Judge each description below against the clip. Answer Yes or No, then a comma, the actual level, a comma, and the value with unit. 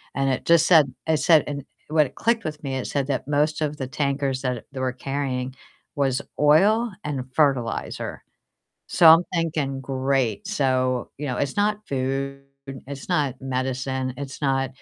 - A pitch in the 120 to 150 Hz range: Yes, medium, 140 Hz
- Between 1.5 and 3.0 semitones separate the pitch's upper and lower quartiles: Yes, narrow, 2.5 semitones